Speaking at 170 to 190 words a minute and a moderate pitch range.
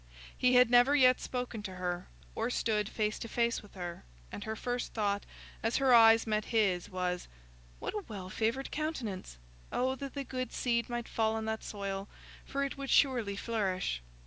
Yes: average, 185 wpm; average, 3.8 semitones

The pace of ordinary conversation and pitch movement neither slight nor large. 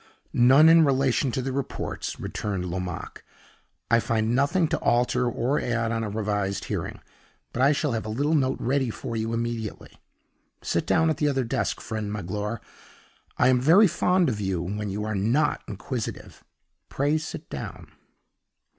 Yes: average, 165 wpm; average, 4.7 semitones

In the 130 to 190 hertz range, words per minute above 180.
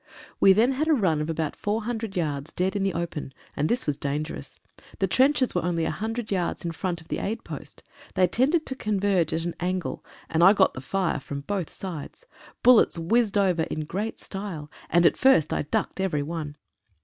Yes: medium, 185 Hz; fast, 205 wpm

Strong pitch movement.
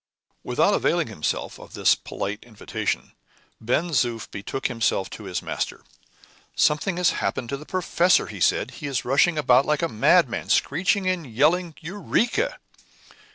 Yes: wide, 6.9 semitones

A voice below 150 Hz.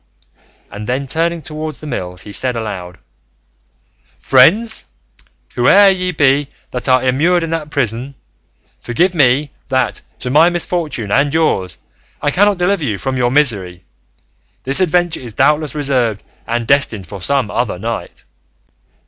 Yes: low, 135 Hz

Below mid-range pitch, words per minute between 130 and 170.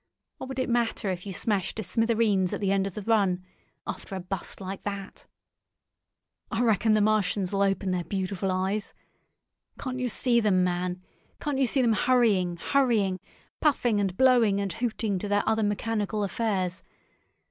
No: high, 205 Hz; average, 165 wpm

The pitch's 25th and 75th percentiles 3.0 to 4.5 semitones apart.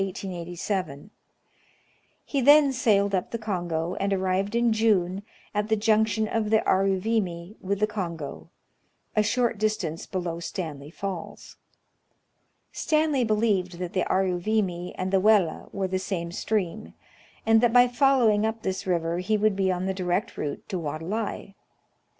Yes: average, 3.5 semitones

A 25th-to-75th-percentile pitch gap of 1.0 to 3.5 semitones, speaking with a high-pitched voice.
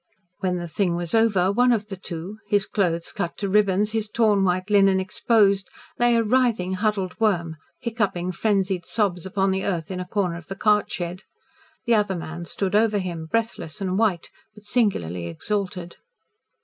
Yes: average, 3.0 semitones; high, 195 Hz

